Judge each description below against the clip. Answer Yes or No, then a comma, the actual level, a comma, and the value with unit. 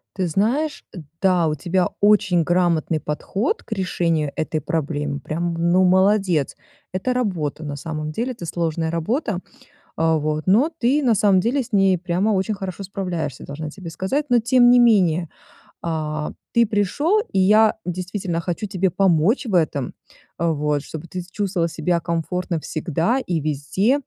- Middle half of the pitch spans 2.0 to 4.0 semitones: No, average, 4.4 semitones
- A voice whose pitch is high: No, medium, 180 Hz